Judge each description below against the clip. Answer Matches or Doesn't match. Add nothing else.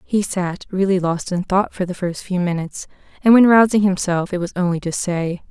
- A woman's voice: Matches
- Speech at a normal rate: Doesn't match